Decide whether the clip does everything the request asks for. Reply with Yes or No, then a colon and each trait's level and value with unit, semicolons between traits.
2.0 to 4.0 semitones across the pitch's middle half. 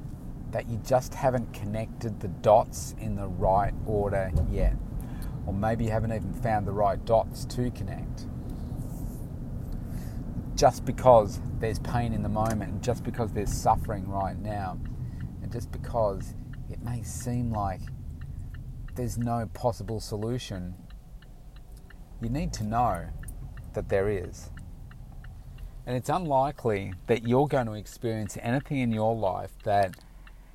Yes: average, 3.4 semitones